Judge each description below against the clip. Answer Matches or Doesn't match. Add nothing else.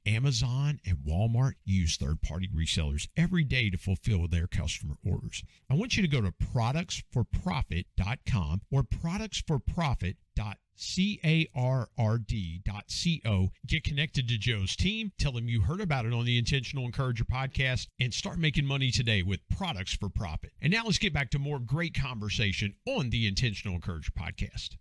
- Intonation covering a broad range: Matches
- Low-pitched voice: Matches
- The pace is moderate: Matches